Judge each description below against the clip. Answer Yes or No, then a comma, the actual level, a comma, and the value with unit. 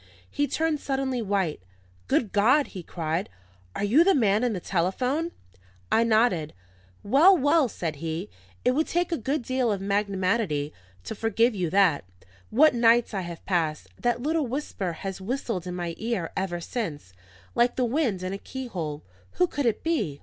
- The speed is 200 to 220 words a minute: No, average, 170 wpm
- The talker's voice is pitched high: Yes, high, 215 Hz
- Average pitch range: No, wide, 6.3 semitones